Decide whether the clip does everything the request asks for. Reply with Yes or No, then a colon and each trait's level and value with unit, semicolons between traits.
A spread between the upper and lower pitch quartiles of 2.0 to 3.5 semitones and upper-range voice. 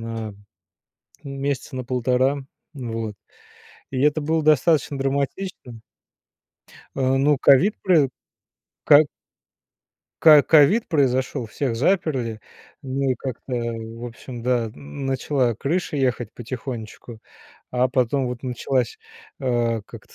No: average, 3.2 semitones; low, 130 Hz